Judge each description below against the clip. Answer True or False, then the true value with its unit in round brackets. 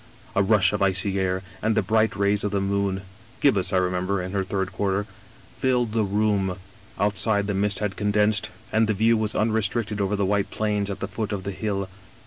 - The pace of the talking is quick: True (215 wpm)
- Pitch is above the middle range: False (100 Hz)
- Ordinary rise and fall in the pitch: False (1.8 semitones)